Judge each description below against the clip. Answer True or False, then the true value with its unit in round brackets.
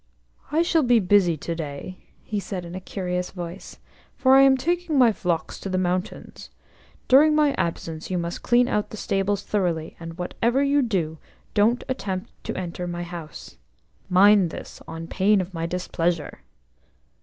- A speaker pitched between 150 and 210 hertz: True (185 Hz)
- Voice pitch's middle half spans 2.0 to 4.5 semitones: False (5.6 semitones)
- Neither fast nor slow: True (165 wpm)